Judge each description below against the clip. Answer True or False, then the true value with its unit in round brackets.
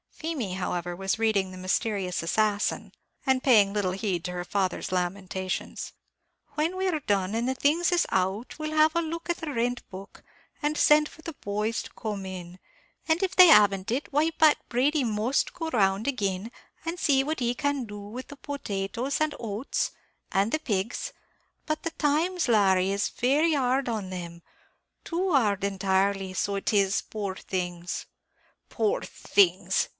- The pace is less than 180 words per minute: True (170 wpm)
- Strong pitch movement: True (7.6 semitones)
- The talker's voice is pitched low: False (220 Hz)